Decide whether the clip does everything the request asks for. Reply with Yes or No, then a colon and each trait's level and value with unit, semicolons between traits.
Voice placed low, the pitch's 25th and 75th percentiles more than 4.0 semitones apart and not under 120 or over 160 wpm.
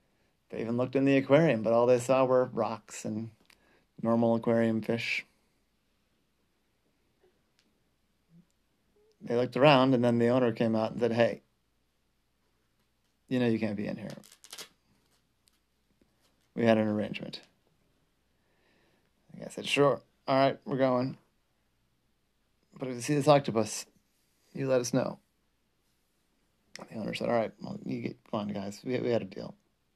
No: low, 120 Hz; average, 2.7 semitones; average, 140 wpm